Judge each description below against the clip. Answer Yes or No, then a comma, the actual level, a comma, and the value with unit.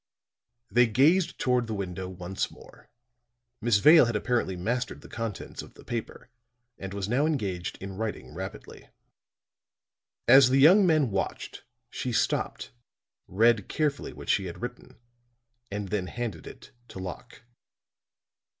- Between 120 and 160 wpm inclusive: Yes, average, 140 wpm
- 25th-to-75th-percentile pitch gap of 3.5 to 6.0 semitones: Yes, average, 4.6 semitones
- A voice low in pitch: Yes, low, 115 Hz